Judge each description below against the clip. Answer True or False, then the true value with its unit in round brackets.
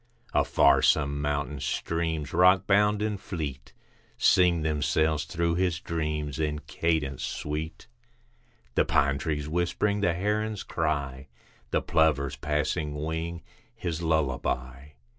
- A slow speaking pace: True (110 wpm)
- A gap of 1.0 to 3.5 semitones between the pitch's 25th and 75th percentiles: True (2.9 semitones)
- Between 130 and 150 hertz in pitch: False (80 Hz)